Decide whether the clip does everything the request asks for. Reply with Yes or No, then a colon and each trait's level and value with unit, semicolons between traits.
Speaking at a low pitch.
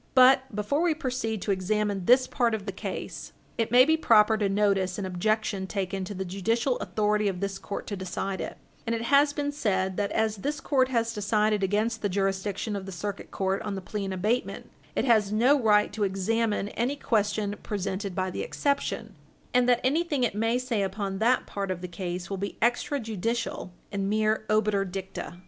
No: high, 210 Hz